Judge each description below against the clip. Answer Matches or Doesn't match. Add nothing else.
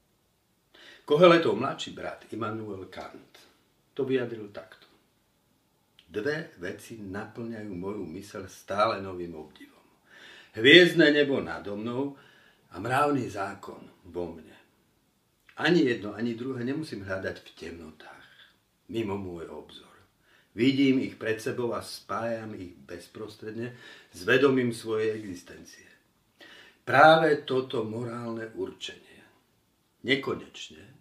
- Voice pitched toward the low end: Matches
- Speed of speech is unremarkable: Doesn't match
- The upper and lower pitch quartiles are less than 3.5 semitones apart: Doesn't match